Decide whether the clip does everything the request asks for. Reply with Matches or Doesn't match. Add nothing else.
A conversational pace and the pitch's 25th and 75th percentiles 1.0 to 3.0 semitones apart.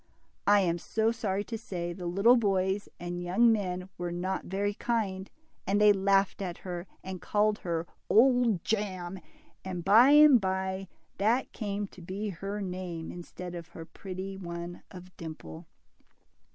Matches